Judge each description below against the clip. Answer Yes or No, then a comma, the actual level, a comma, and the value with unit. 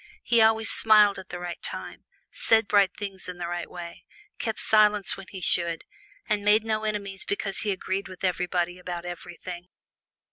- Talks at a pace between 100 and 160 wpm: No, average, 175 wpm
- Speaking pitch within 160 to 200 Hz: Yes, high, 190 Hz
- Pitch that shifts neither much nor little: Yes, average, 3.0 semitones